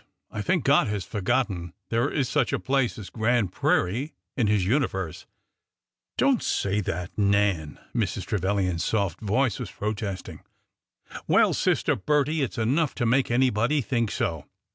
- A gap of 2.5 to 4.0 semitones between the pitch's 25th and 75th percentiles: No, average, 5.3 semitones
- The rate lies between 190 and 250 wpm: No, average, 165 wpm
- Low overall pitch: Yes, low, 110 Hz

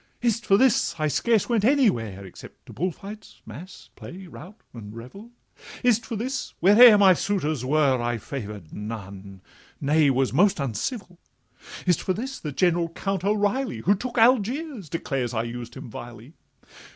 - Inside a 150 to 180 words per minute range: Yes, average, 165 wpm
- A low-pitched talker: No, medium, 175 Hz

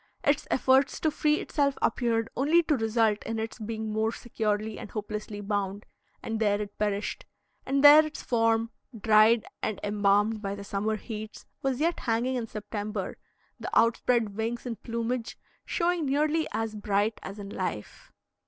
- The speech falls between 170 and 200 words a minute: No, average, 160 wpm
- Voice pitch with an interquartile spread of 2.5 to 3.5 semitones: Yes, average, 3.2 semitones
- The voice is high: Yes, high, 225 Hz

